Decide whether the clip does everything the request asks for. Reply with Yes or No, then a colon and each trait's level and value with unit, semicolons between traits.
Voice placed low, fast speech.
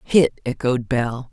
No: low, 130 Hz; slow, 135 wpm